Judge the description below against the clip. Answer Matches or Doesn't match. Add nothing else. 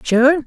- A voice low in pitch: Doesn't match